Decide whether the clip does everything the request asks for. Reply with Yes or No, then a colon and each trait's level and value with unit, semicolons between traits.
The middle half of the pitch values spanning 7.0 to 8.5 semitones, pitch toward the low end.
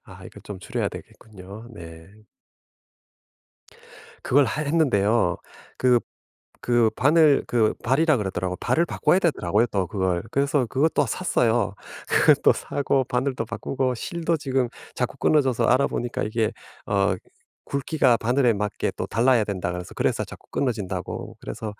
No: average, 5.3 semitones; low, 120 Hz